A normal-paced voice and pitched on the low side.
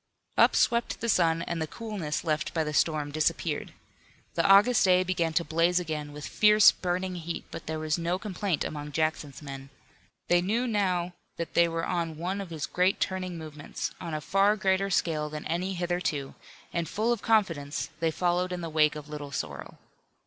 No: average, 190 wpm; medium, 170 Hz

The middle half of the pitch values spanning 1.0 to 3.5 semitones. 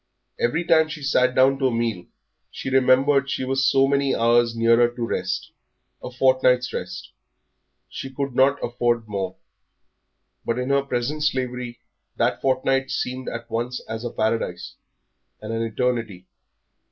Yes: narrow, 2.4 semitones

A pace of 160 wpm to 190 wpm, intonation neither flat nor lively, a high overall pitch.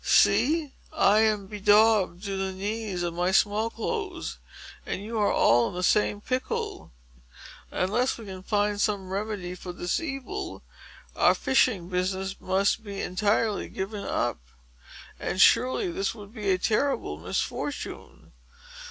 No: average, 140 wpm; average, 3.2 semitones; high, 205 Hz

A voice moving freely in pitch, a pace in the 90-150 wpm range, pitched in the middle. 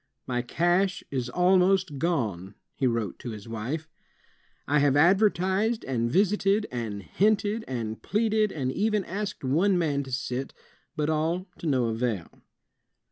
Yes: wide, 7.7 semitones; average, 140 wpm; medium, 155 Hz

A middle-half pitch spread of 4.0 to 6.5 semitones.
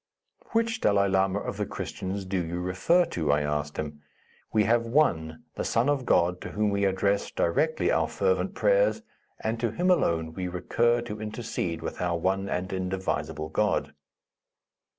Yes: average, 5.2 semitones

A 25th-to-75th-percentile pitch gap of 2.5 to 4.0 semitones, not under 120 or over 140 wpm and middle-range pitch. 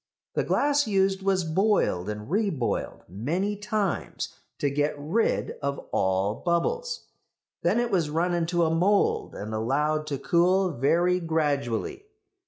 No: wide, 5.5 semitones; slow, 135 wpm; medium, 170 Hz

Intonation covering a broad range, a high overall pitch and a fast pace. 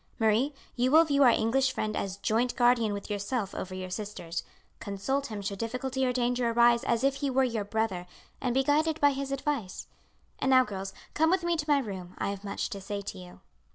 No: average, 5.0 semitones; high, 235 Hz; fast, 220 wpm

